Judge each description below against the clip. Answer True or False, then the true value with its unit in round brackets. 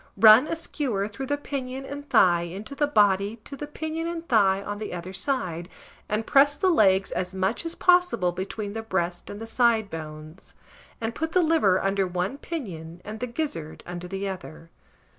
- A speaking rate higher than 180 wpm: True (190 wpm)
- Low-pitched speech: False (210 Hz)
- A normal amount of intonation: False (7.1 semitones)